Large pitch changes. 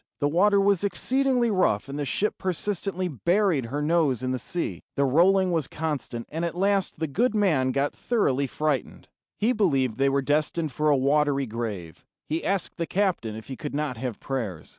Yes: wide, 6.0 semitones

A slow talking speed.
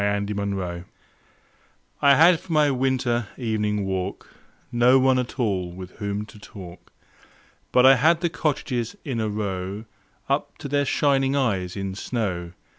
No: average, 150 wpm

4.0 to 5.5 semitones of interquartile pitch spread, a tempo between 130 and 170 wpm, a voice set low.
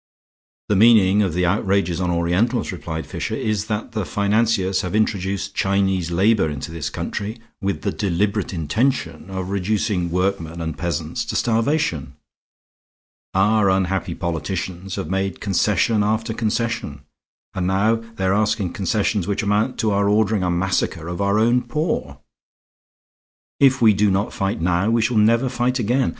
No: average, 3.3 semitones; average, 155 wpm; low, 100 Hz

